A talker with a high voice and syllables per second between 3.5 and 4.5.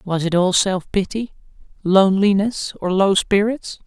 Yes: high, 195 Hz; 4.4 syllables/s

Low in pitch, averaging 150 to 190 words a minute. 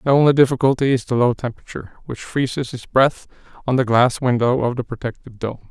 No: low, 125 Hz; average, 200 wpm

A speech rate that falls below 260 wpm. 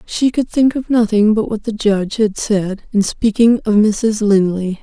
Yes: average, 200 wpm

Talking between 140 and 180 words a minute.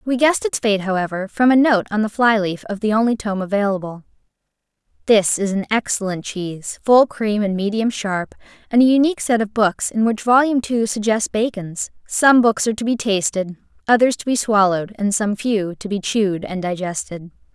No: average, 190 wpm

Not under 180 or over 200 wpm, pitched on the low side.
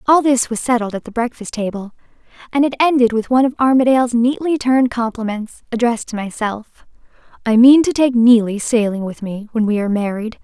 No: average, 190 wpm; high, 235 Hz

